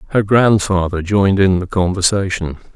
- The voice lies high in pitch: No, very low, 95 Hz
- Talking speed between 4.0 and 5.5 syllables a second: Yes, 5.2 syllables/s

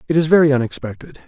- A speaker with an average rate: Yes, average, 190 wpm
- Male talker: Yes, male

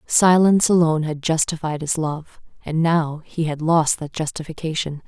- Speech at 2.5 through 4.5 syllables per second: No, 4.9 syllables/s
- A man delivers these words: No, female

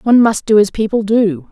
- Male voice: No, female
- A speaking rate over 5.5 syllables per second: Yes, 5.7 syllables/s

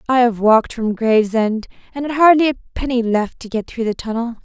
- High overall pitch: Yes, high, 235 Hz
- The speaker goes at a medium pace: No, fast, 215 wpm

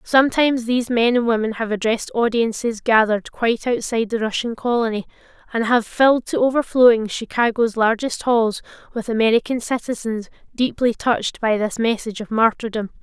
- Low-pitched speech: No, high, 230 Hz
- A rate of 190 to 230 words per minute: No, average, 145 wpm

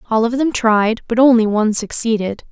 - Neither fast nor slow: Yes, average, 190 wpm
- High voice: Yes, high, 225 Hz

